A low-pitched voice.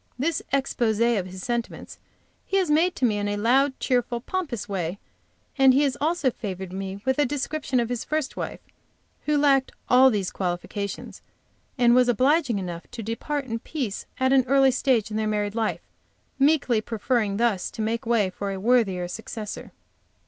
No: high, 235 Hz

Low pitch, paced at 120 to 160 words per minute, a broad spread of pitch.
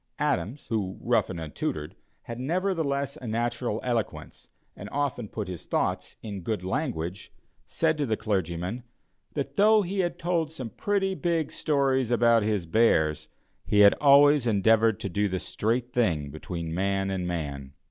Yes: low, 115 Hz; average, 155 wpm; wide, 7.2 semitones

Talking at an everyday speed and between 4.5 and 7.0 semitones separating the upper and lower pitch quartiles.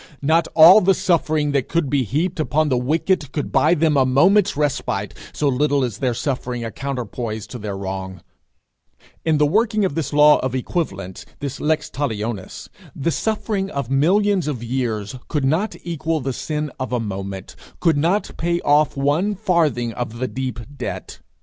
Yes: average, 175 wpm; average, 5.0 semitones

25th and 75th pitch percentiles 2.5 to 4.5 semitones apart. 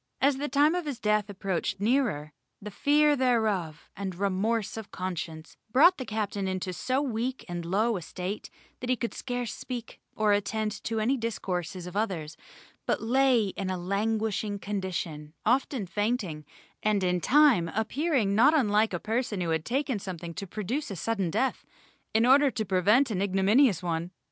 No: average, 4.9 semitones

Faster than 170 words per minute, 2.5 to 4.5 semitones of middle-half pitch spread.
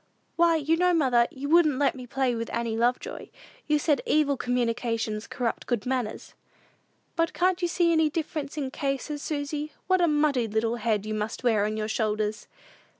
No: average, 185 wpm; average, 5.1 semitones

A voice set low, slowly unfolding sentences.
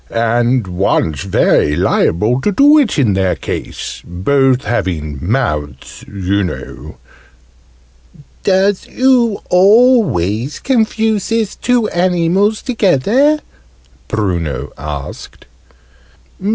Yes: low, 130 Hz; slow, 90 wpm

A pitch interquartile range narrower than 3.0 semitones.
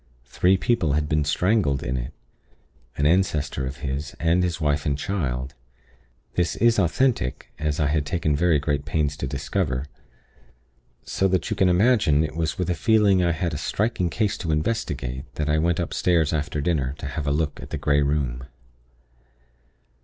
No: average, 3.9 semitones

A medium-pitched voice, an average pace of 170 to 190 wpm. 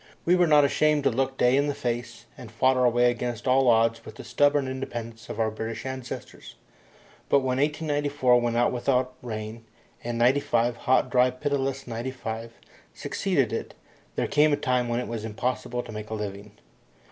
No: low, 125 Hz; average, 180 wpm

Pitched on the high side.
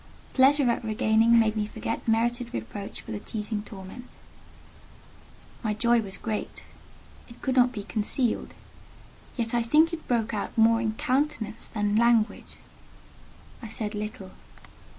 Yes: high, 225 Hz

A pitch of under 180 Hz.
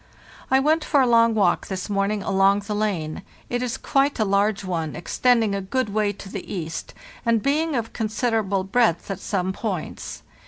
No: high, 210 Hz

